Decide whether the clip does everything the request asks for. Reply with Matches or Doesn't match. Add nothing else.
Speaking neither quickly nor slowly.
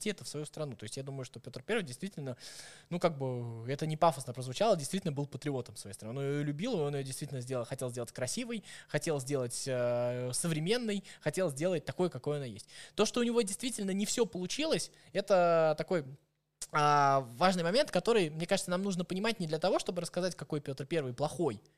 Doesn't match